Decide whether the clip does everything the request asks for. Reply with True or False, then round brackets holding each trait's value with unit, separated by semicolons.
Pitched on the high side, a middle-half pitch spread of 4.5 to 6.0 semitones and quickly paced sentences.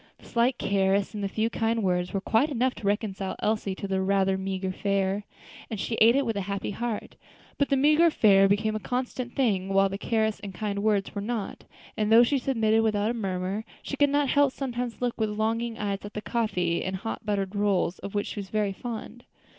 False (210 Hz; 3.1 semitones; 220 wpm)